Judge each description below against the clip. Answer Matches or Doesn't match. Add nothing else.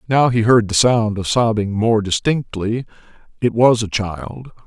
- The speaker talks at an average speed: Matches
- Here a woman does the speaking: Doesn't match